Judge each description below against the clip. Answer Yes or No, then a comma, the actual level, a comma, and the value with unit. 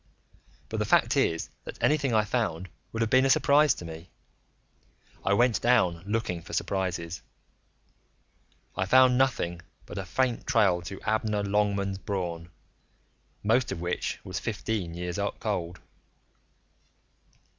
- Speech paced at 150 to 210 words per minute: No, slow, 135 wpm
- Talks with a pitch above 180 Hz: No, low, 100 Hz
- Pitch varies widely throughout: No, average, 4.8 semitones